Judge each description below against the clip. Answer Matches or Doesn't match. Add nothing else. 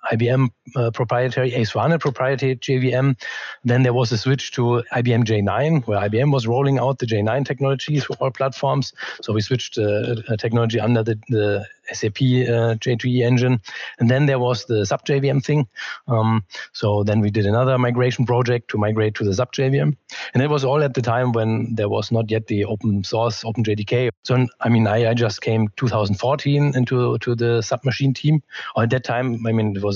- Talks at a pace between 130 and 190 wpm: Doesn't match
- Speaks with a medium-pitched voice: Doesn't match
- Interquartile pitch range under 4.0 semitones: Matches